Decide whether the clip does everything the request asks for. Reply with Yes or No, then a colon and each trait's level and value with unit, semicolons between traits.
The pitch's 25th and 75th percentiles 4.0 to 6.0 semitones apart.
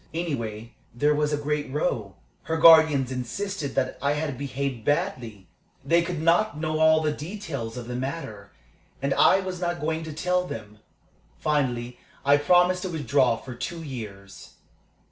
Yes: average, 4.9 semitones